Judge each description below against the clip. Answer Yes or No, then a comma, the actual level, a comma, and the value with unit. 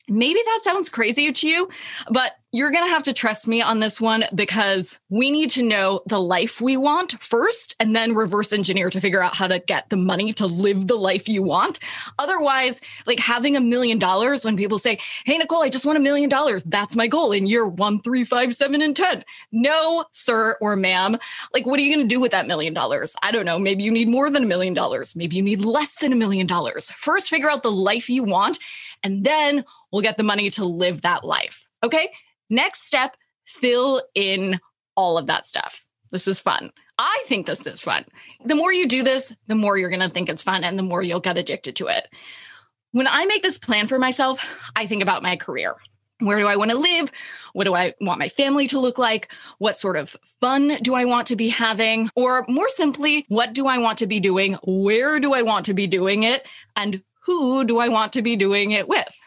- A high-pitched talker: Yes, high, 230 Hz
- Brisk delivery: Yes, fast, 230 wpm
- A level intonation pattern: No, wide, 5.6 semitones